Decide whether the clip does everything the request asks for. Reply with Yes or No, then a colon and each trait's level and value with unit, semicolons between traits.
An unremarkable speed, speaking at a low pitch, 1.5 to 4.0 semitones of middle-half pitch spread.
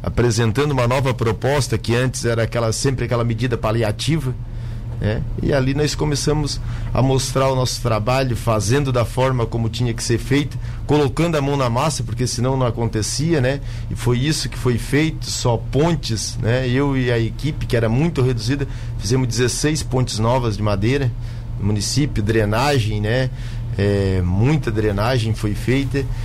Yes: average, 165 wpm; low, 120 Hz; narrow, 2.5 semitones